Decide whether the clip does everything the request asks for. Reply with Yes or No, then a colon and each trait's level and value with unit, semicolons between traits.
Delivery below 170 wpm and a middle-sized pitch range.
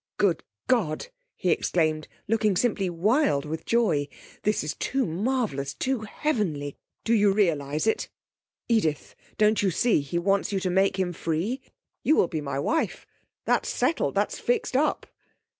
No: average, 155 wpm; wide, 6.4 semitones